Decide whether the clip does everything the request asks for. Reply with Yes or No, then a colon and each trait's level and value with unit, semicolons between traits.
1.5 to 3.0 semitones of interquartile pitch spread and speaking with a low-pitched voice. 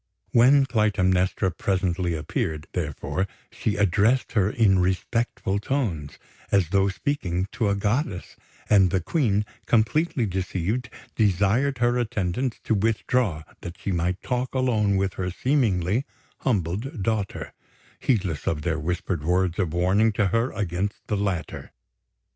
No: average, 4.3 semitones; low, 100 Hz